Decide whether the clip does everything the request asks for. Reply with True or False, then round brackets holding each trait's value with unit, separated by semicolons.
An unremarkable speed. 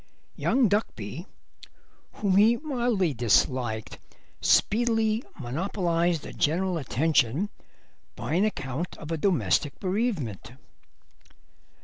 False (90 wpm)